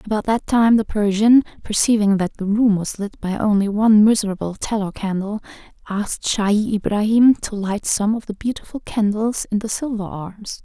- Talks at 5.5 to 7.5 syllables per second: No, 5.0 syllables/s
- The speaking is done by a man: No, female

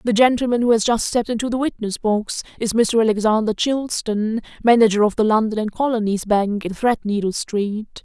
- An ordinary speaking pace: Yes, average, 180 wpm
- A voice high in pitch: Yes, high, 220 Hz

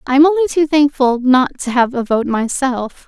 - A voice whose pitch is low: No, very high, 270 Hz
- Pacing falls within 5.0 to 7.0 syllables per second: Yes, 5.1 syllables/s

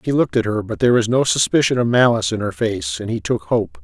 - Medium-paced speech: No, fast, 280 wpm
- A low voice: Yes, low, 120 Hz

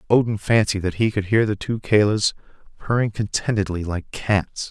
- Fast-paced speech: No, average, 165 wpm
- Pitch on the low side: Yes, low, 105 Hz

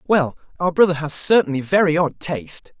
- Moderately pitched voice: Yes, medium, 165 Hz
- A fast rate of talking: No, average, 170 wpm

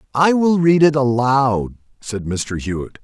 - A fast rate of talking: No, average, 160 wpm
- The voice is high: No, low, 130 Hz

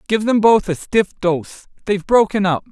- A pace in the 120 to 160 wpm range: No, average, 200 wpm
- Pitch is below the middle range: No, high, 195 Hz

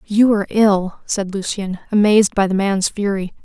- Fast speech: No, average, 175 wpm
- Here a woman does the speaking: Yes, female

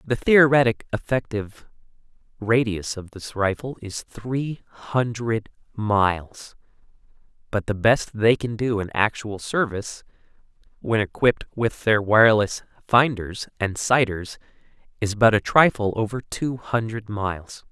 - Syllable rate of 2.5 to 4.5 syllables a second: Yes, 4.3 syllables/s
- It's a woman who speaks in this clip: No, male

